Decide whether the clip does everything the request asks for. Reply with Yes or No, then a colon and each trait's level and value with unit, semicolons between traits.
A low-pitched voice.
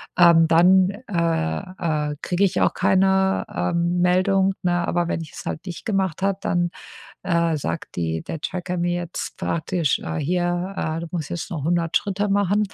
No: medium, 175 Hz